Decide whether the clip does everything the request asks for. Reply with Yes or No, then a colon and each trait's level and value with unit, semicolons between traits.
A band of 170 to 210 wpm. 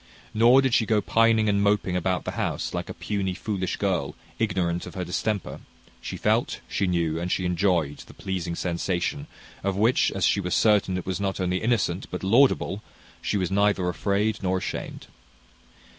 Yes: average, 180 wpm